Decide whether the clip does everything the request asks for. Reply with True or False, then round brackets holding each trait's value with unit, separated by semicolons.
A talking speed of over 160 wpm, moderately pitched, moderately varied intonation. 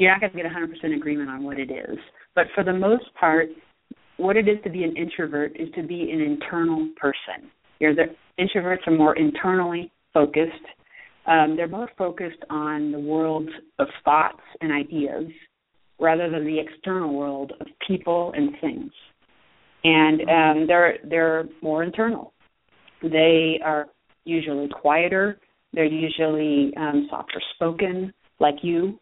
False (150 wpm; 165 Hz; 3.2 semitones)